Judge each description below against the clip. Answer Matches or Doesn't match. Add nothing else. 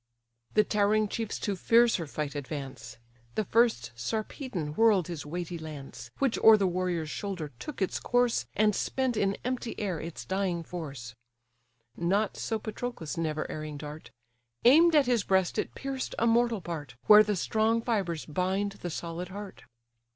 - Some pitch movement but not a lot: Doesn't match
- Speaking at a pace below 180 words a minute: Matches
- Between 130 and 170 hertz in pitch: Doesn't match